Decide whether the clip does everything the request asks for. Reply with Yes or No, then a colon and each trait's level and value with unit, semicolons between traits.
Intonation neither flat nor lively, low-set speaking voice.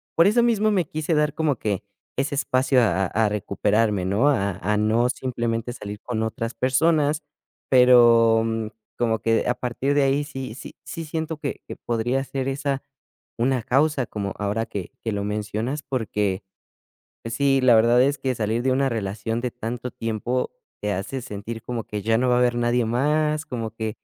Yes: average, 3.7 semitones; low, 120 Hz